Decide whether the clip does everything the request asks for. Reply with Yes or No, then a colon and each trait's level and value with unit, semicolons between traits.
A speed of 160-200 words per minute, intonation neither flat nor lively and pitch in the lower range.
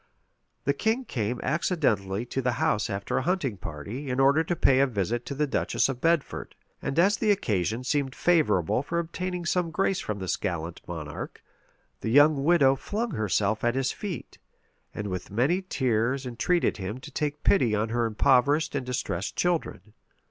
No: average, 175 wpm; wide, 7.0 semitones; low, 130 Hz